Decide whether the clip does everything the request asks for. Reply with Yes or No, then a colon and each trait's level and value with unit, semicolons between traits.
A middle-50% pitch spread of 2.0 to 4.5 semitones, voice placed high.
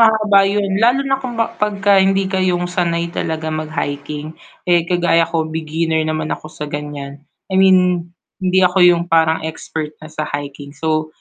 No: average, 3.5 semitones; medium, 165 Hz